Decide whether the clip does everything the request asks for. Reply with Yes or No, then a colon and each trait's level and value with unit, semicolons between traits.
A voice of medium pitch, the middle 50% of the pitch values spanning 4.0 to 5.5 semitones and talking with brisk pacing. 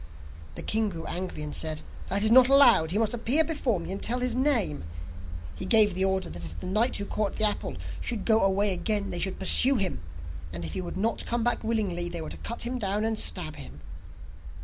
No: high, 205 Hz; average, 4.7 semitones; fast, 230 wpm